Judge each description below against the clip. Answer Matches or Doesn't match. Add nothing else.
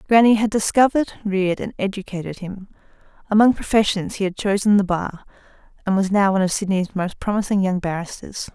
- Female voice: Matches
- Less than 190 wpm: Matches